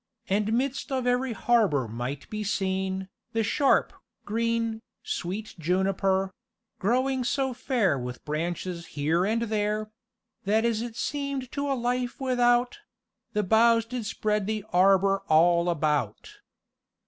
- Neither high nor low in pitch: No, high, 215 Hz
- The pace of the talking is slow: Yes, slow, 130 wpm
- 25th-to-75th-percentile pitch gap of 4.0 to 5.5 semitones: Yes, average, 4.6 semitones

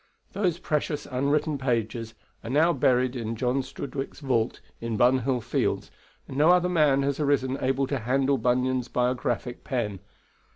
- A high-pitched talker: No, low, 130 Hz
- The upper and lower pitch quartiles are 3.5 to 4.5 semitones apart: No, narrow, 2.4 semitones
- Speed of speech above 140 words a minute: Yes, average, 150 wpm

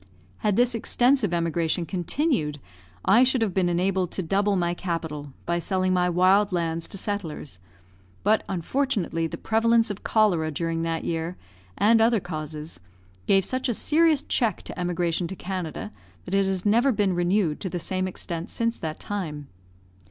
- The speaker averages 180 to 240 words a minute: No, average, 165 wpm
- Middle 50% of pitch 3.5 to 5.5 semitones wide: Yes, average, 4.1 semitones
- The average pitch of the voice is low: No, medium, 185 Hz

